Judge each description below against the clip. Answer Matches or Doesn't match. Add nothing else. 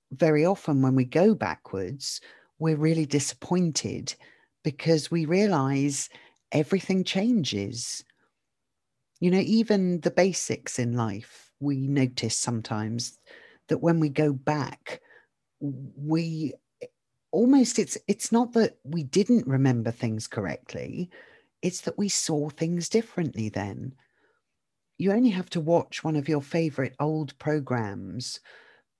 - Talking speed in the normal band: Doesn't match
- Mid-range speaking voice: Matches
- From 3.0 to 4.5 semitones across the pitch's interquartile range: Doesn't match